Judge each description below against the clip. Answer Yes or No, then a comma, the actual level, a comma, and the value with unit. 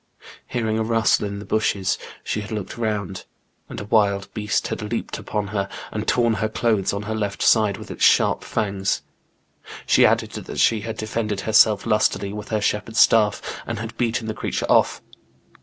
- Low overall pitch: Yes, low, 105 Hz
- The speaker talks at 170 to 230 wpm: Yes, average, 185 wpm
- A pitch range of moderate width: No, narrow, 1.5 semitones